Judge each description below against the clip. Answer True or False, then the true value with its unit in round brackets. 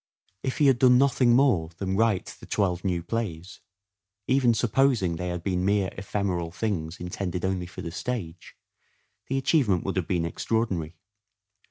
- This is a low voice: True (95 Hz)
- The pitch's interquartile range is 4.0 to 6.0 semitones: True (5.0 semitones)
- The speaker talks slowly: False (160 wpm)